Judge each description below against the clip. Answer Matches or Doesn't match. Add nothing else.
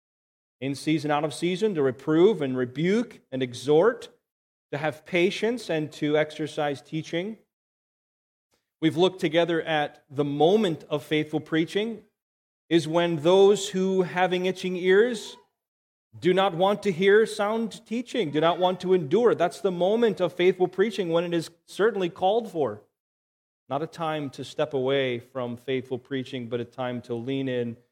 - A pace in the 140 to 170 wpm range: Matches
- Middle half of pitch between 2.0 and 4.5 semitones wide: Doesn't match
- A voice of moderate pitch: Matches